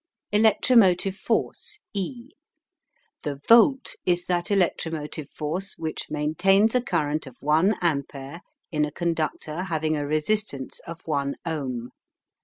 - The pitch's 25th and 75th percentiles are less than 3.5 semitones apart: No, average, 4.6 semitones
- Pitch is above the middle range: No, medium, 165 Hz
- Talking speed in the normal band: No, slow, 120 wpm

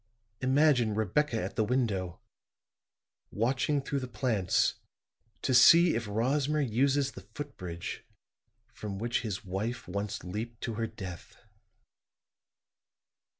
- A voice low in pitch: Yes, low, 115 Hz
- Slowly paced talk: Yes, slow, 110 wpm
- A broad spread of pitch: No, average, 4.6 semitones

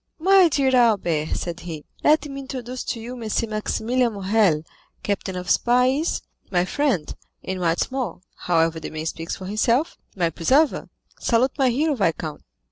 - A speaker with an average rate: Yes, average, 150 wpm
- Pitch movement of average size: No, wide, 6.9 semitones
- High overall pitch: Yes, high, 220 Hz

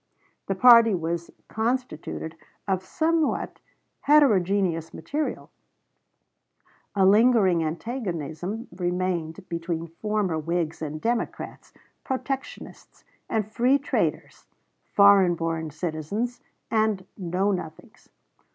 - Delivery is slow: Yes, slow, 85 wpm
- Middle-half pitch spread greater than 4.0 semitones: Yes, average, 5.3 semitones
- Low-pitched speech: No, high, 190 Hz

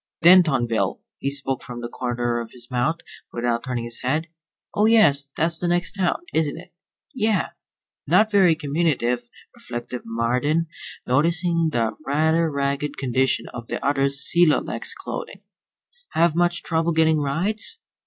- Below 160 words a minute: Yes, average, 145 wpm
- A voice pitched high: No, medium, 145 Hz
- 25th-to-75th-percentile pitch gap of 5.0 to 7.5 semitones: Yes, average, 5.3 semitones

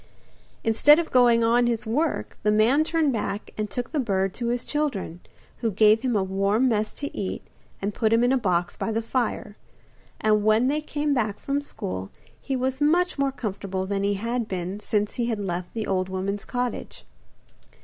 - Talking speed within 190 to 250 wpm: Yes, average, 195 wpm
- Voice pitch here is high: Yes, high, 225 Hz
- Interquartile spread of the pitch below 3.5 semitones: No, average, 4.2 semitones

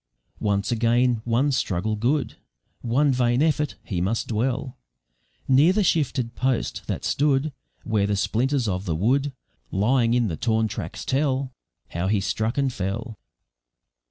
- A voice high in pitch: No, low, 120 Hz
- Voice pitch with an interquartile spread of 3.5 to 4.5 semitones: Yes, average, 4.0 semitones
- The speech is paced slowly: No, average, 145 wpm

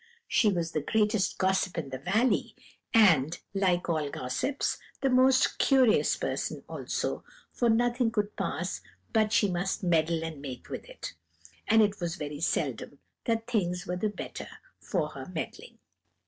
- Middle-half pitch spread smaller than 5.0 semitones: No, average, 5.3 semitones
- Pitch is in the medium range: No, high, 195 Hz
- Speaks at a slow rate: No, average, 155 wpm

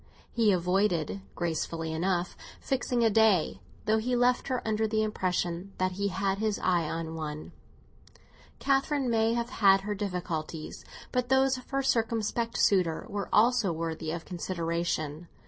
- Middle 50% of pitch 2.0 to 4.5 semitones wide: No, average, 5.1 semitones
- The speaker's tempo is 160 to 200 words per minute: No, average, 145 wpm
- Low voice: No, high, 195 Hz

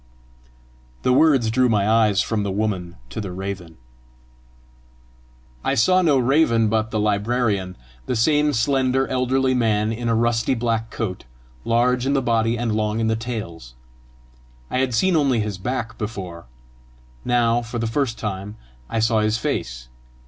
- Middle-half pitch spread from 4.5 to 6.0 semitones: No, average, 2.9 semitones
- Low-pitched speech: Yes, low, 115 Hz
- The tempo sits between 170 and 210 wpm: No, average, 155 wpm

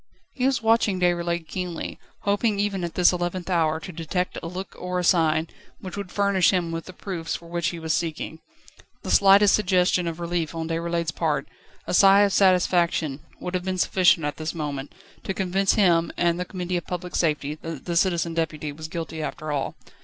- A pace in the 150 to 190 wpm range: No, average, 200 wpm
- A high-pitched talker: No, medium, 175 Hz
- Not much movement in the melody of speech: Yes, narrow, 2.3 semitones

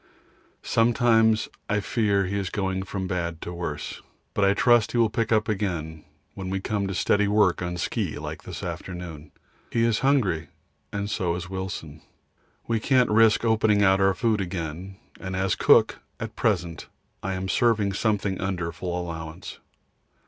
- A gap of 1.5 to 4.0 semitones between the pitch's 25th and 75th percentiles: Yes, average, 3.5 semitones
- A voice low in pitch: Yes, very low, 95 Hz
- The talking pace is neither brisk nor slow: Yes, average, 165 wpm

